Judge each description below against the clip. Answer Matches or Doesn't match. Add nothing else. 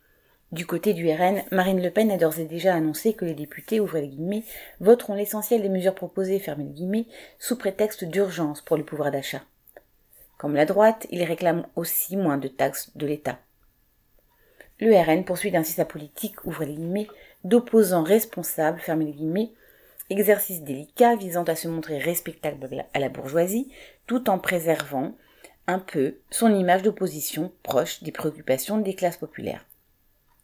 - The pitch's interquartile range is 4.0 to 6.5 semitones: Matches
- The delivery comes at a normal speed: Matches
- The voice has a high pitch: Doesn't match